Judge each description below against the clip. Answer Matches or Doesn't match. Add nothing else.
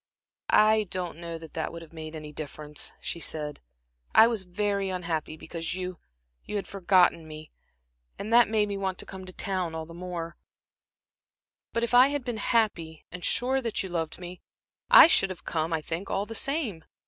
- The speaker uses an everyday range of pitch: Matches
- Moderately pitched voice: Matches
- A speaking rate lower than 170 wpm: Doesn't match